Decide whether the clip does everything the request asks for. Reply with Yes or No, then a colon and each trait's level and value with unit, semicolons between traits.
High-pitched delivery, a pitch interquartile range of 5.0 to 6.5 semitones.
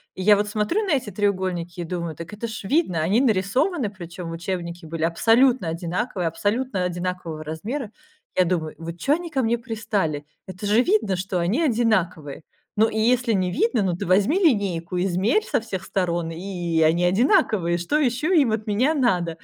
Yes: high, 195 Hz; average, 5.3 semitones